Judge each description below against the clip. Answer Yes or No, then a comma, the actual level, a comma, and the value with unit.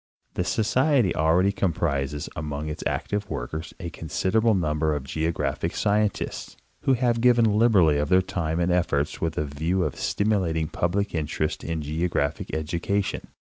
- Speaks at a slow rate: No, average, 145 wpm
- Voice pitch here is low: Yes, very low, 85 Hz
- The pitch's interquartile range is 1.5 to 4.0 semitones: No, average, 4.8 semitones